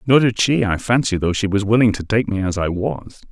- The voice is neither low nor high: No, low, 105 Hz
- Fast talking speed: Yes, fast, 270 wpm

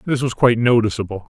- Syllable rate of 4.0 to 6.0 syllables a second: No, 6.8 syllables/s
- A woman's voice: No, male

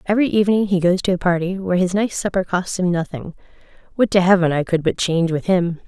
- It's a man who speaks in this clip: No, female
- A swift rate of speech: Yes, fast, 235 wpm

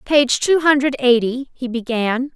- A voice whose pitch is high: Yes, very high, 260 Hz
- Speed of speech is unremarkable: Yes, average, 155 wpm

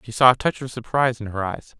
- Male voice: Yes, male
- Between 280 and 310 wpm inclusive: Yes, fast, 300 wpm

